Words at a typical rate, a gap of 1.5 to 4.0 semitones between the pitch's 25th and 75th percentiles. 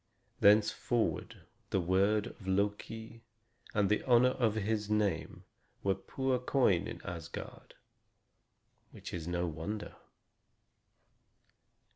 No: slow, 100 wpm; average, 3.1 semitones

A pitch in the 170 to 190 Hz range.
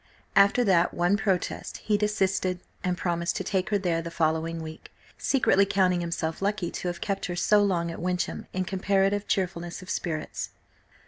Yes: medium, 185 Hz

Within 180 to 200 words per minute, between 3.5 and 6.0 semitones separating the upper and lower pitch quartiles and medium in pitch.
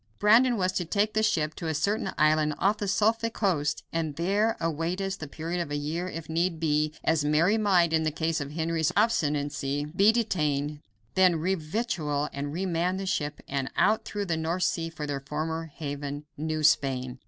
Yes: average, 195 wpm; average, 4.0 semitones; medium, 160 Hz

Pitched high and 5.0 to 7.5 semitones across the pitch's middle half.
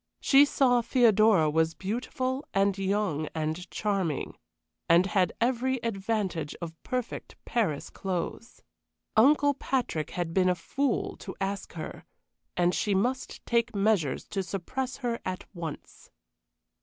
Yes: high, 200 Hz; wide, 5.5 semitones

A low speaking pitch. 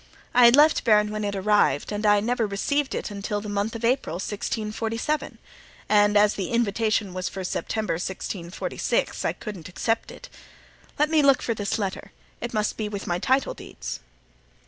No: high, 210 Hz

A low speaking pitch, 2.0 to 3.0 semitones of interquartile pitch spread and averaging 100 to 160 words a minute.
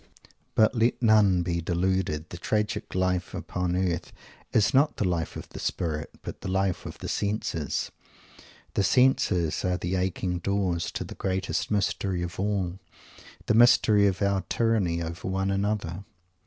Yes: very low, 95 Hz; average, 2.7 semitones; average, 155 wpm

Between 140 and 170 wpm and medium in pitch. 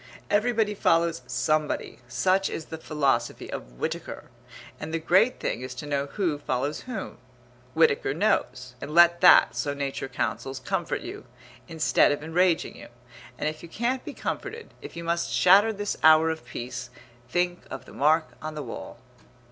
Yes: average, 165 wpm; medium, 160 Hz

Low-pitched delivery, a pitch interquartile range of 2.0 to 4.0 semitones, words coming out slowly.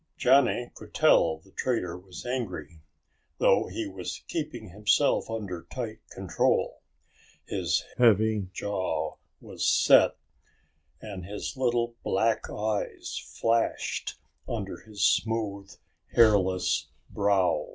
Yes: low, 105 Hz; average, 3.7 semitones; slow, 105 wpm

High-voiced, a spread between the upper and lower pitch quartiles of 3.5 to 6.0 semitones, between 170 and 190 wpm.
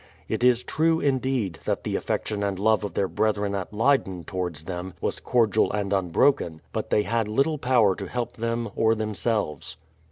No: low, 110 Hz; average, 4.1 semitones; average, 180 wpm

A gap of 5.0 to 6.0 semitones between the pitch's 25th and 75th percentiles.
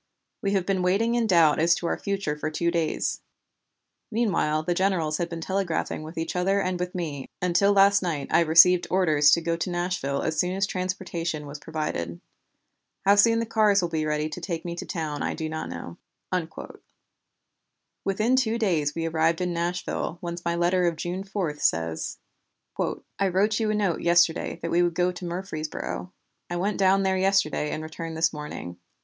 No: average, 3.2 semitones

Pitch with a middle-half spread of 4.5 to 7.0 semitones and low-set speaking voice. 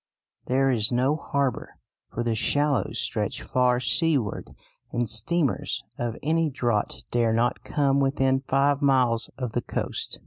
No: average, 2.9 semitones; low, 130 Hz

